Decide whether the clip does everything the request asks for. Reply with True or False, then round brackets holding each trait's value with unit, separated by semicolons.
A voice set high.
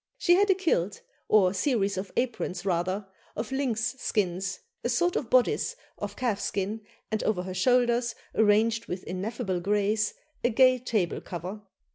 True (215 Hz)